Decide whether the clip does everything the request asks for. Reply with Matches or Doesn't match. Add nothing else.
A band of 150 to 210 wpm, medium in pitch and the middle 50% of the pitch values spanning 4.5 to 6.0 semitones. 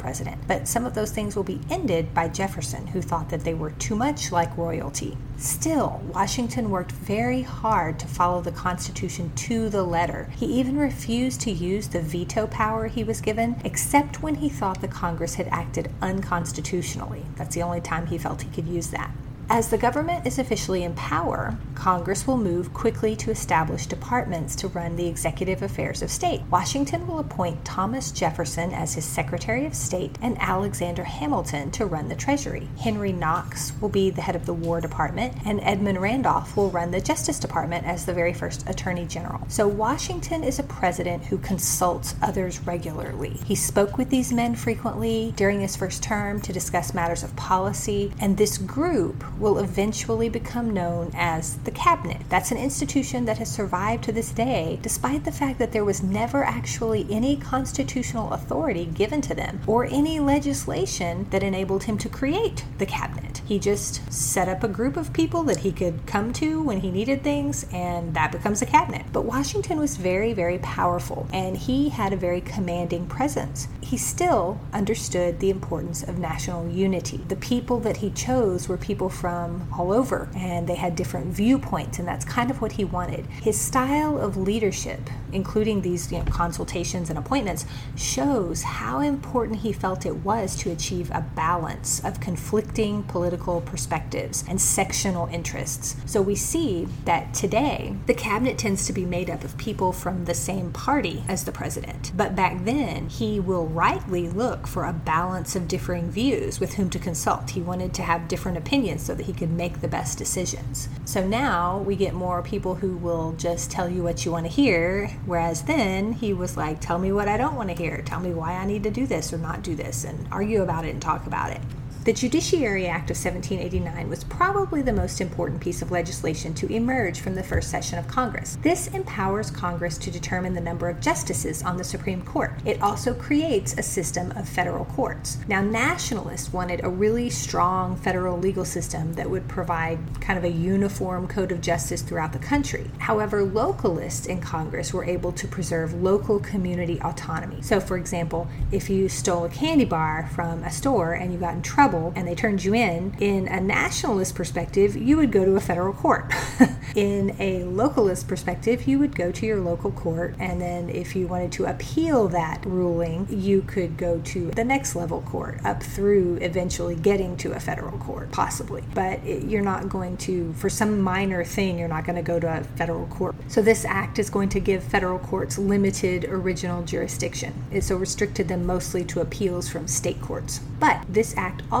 Matches